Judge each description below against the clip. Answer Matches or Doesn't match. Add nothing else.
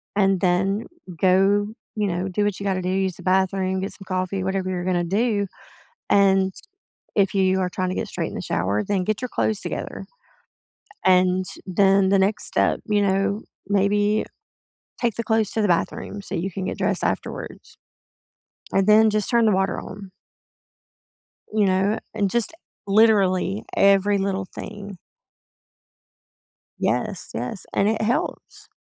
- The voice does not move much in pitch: Matches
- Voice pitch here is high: Matches